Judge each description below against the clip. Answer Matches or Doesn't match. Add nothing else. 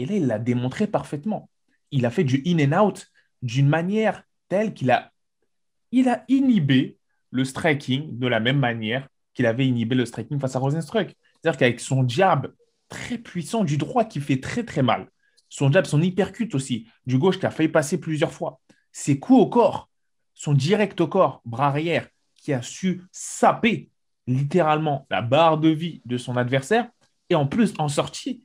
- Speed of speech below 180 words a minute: Doesn't match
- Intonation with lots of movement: Matches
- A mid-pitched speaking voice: Matches